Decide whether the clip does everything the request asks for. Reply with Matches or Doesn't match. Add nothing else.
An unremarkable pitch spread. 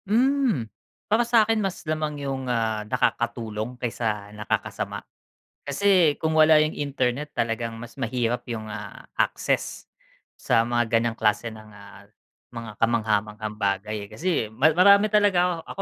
Doesn't match